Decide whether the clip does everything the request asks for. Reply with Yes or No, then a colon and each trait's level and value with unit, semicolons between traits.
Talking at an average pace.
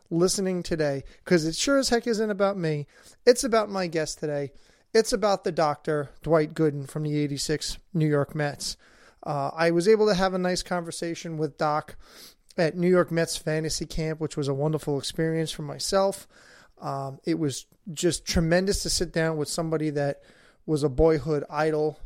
Yes: average, 180 wpm